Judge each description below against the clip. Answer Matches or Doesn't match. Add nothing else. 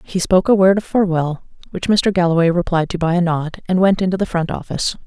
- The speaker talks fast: Matches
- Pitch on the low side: Doesn't match